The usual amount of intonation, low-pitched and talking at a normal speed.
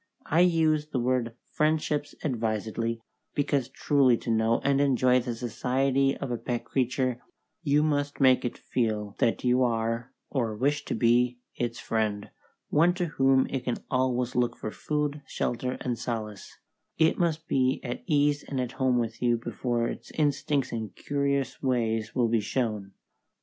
Yes: average, 3.4 semitones; low, 125 Hz; average, 160 wpm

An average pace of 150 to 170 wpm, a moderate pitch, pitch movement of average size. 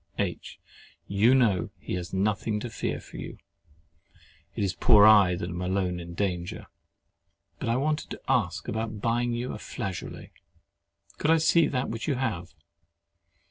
No: average, 155 wpm; low, 105 Hz; average, 4.9 semitones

